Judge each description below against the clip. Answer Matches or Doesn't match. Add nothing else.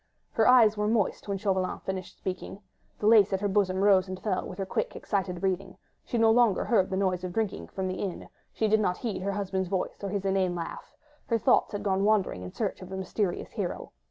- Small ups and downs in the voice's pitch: Matches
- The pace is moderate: Doesn't match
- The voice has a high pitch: Matches